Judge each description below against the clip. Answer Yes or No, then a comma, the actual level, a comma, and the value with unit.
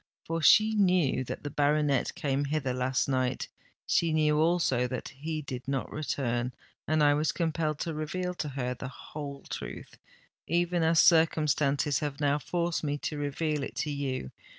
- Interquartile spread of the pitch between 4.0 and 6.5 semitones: No, average, 2.9 semitones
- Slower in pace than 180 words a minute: Yes, average, 160 wpm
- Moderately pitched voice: Yes, medium, 150 Hz